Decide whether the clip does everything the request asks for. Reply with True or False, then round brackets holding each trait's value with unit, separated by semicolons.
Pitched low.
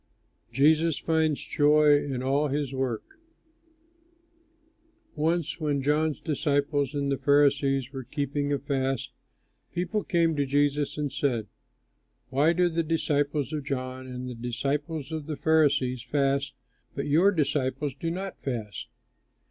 False (145 Hz)